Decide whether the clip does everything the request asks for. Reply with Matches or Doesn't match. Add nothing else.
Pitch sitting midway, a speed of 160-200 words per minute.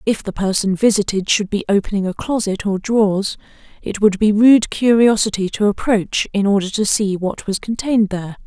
Doesn't match